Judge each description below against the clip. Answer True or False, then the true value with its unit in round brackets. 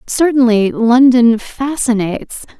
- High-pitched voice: True (245 Hz)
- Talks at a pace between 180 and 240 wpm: False (70 wpm)